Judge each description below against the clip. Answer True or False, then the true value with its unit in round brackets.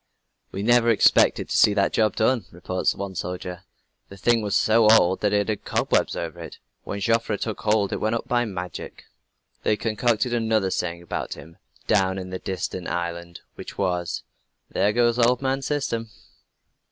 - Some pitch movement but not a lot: True (3.8 semitones)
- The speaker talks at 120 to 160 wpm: False (175 wpm)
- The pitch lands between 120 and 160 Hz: False (105 Hz)